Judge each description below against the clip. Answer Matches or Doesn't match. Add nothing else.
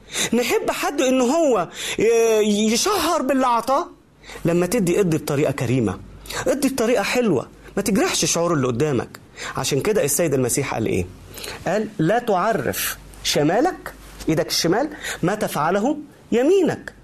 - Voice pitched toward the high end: Matches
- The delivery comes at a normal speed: Matches